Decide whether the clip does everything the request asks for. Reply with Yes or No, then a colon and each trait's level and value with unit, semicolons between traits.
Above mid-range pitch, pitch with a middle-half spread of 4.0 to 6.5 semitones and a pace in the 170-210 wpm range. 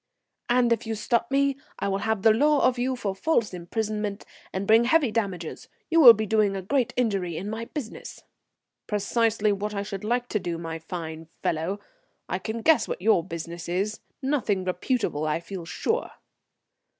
Yes: high, 210 Hz; average, 4.3 semitones; average, 185 wpm